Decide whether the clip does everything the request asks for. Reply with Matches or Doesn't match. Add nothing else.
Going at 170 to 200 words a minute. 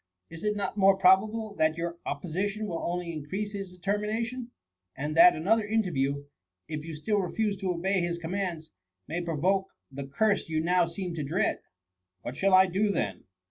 Matches